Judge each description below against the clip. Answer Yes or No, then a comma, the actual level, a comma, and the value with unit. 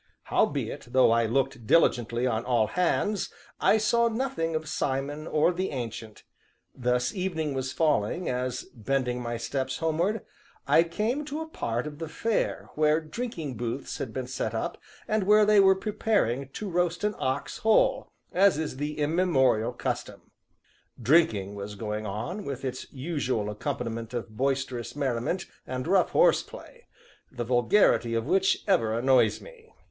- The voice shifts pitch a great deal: Yes, wide, 7.0 semitones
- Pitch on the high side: No, medium, 140 Hz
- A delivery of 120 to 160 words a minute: Yes, average, 155 wpm